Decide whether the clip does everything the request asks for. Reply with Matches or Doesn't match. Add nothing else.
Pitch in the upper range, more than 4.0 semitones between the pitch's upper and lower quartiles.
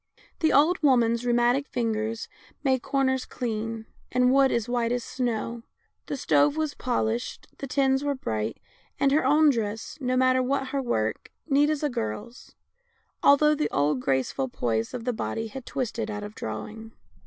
Doesn't match